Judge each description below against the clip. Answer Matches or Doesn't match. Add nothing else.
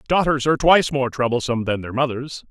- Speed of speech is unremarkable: Matches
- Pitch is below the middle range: Matches